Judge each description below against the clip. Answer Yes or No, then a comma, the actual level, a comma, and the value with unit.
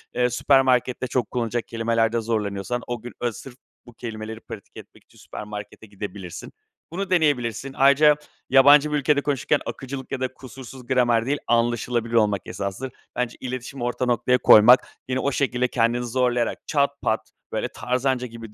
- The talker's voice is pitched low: Yes, low, 125 Hz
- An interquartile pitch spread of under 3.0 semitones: Yes, narrow, 2.5 semitones